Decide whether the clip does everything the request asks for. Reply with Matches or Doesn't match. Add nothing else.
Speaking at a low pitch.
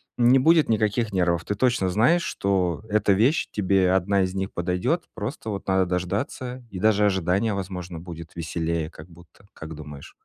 Matches